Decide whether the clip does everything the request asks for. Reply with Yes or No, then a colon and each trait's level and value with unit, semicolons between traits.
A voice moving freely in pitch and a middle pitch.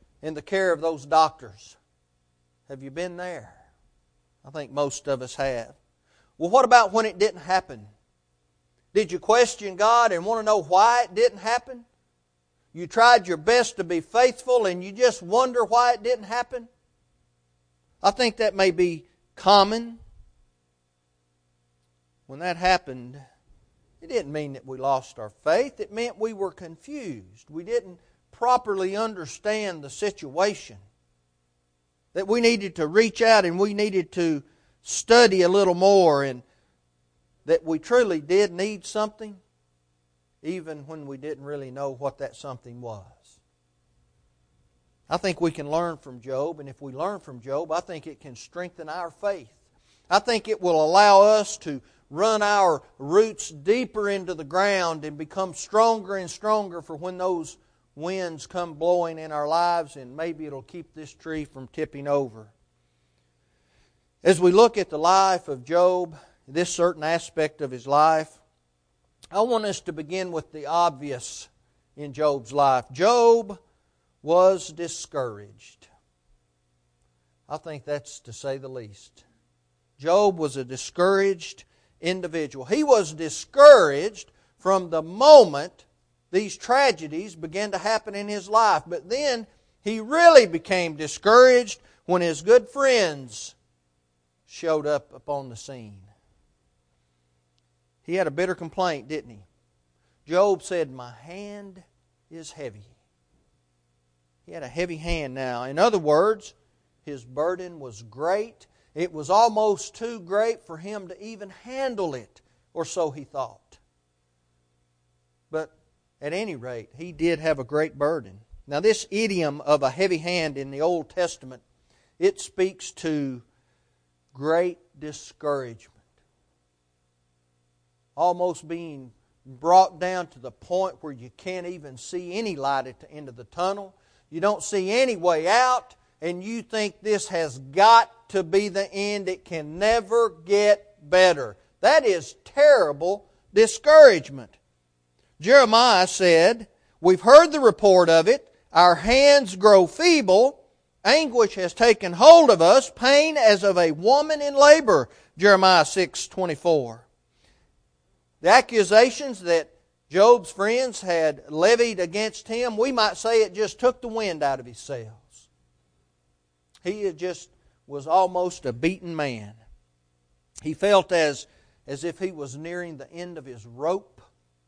Yes: wide, 8.8 semitones; medium, 165 Hz